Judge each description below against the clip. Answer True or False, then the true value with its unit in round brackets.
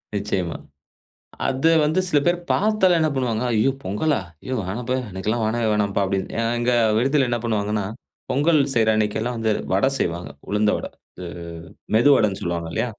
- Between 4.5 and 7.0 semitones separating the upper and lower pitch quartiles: True (4.8 semitones)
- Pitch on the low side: True (110 Hz)